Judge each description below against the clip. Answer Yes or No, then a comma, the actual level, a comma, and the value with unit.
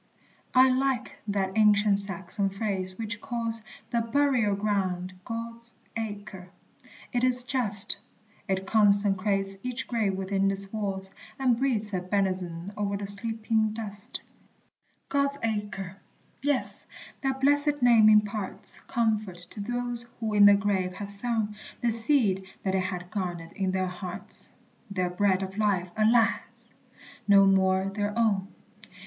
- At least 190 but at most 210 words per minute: No, slow, 135 wpm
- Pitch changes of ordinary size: Yes, average, 3.0 semitones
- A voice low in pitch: No, high, 205 Hz